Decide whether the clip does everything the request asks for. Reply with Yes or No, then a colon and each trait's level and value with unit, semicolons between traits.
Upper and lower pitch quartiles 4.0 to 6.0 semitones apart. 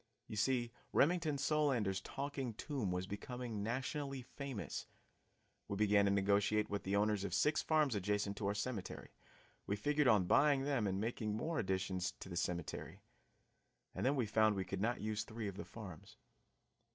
Yes: average, 5.1 semitones